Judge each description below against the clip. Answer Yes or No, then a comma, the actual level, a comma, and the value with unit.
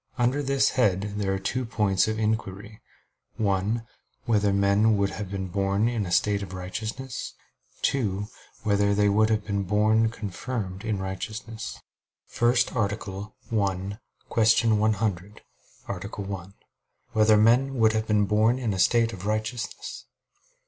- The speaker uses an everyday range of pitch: No, narrow, 2.3 semitones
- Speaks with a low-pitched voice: Yes, low, 105 Hz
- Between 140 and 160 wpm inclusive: Yes, average, 145 wpm